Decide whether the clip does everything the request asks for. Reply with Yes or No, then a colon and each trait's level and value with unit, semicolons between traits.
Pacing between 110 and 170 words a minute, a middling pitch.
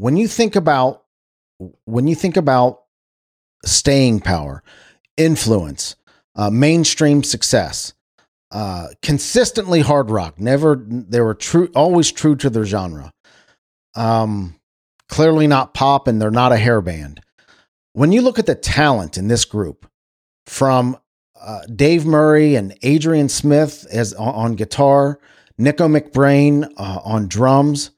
No: slow, 135 wpm; low, 130 Hz